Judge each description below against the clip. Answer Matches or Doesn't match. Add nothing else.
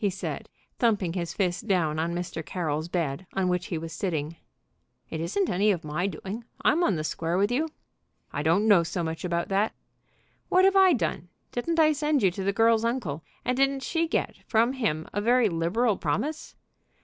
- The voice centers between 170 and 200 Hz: Matches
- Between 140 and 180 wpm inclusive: Doesn't match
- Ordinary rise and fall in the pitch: Doesn't match